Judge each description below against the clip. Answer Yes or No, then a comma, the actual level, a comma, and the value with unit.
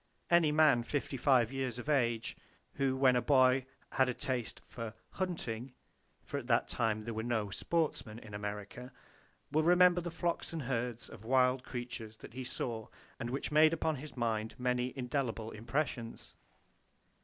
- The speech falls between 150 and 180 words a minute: Yes, average, 155 wpm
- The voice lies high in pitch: No, low, 125 Hz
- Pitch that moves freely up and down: No, average, 3.7 semitones